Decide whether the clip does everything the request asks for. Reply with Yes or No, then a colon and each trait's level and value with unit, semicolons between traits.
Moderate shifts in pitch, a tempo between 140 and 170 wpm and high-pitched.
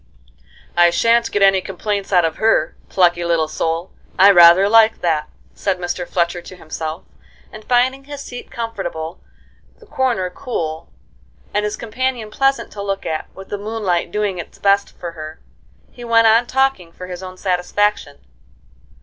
Yes: average, 4.7 semitones; average, 160 wpm; high, 195 Hz